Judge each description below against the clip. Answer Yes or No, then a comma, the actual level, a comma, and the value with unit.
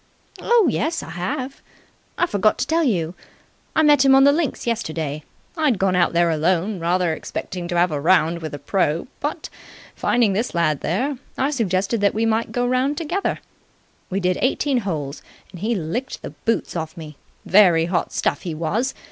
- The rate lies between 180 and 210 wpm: Yes, average, 185 wpm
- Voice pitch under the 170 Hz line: No, high, 195 Hz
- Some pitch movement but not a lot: No, wide, 7.3 semitones